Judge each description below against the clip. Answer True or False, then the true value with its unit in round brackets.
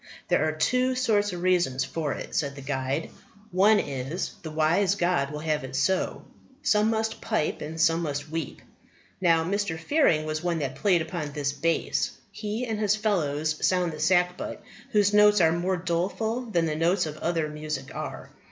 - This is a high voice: False (165 Hz)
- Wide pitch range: False (4.8 semitones)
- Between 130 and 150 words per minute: False (180 wpm)